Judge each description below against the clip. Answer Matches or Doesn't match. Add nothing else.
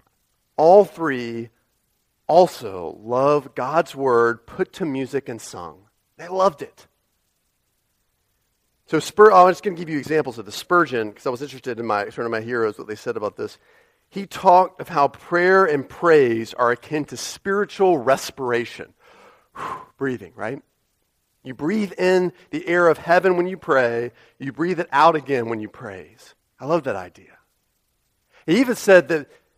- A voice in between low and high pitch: Matches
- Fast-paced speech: Doesn't match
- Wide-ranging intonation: Matches